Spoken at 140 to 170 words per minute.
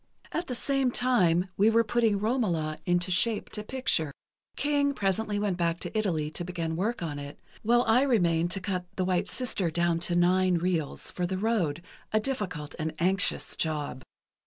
No: average, 180 wpm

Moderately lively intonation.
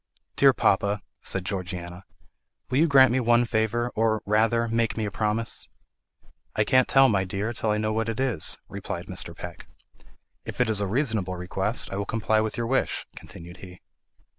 Yes: average, 3.2 semitones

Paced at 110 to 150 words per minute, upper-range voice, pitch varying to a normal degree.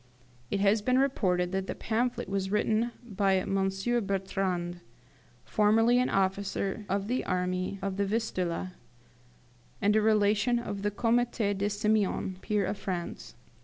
No: average, 140 wpm; high, 200 Hz; narrow, 2.2 semitones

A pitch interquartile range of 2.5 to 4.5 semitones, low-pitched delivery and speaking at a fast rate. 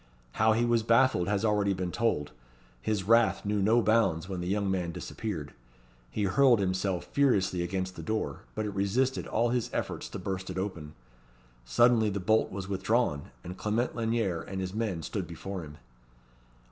No: average, 3.4 semitones; low, 100 Hz; average, 175 wpm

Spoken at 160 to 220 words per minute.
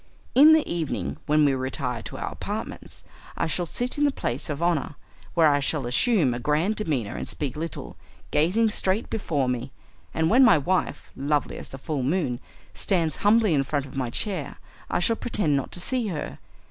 Yes: average, 195 wpm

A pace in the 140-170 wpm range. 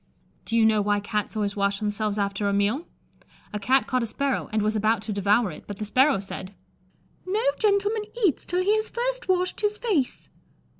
No: average, 200 wpm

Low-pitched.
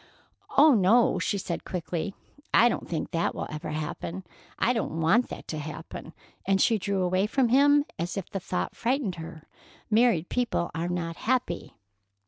No: high, 190 Hz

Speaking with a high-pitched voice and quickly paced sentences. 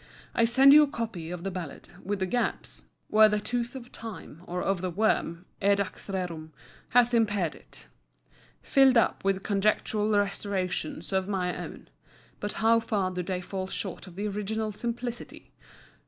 No: high, 200 Hz; average, 165 wpm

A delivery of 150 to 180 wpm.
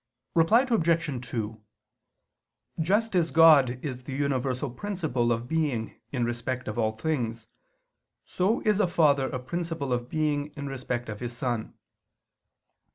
No: average, 140 wpm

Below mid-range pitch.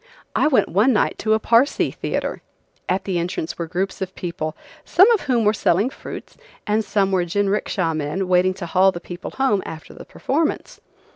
No: high, 195 Hz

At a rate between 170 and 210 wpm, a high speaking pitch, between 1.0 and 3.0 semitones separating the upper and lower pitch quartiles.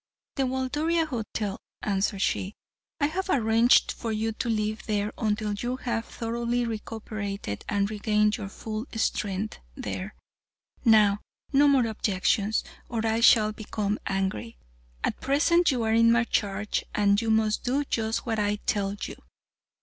No: average, 145 wpm; high, 220 Hz; narrow, 2.4 semitones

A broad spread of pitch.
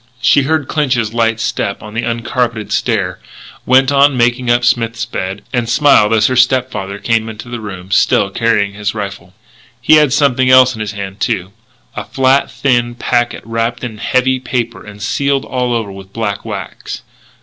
No: average, 3.3 semitones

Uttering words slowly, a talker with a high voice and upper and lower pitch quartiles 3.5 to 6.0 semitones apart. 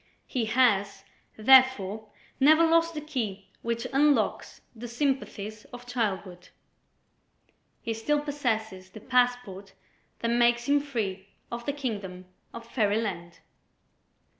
Yes: slow, 115 wpm; high, 235 Hz; average, 4.6 semitones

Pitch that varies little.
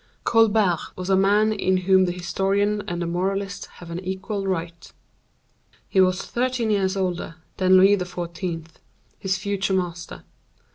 Yes: narrow, 2.1 semitones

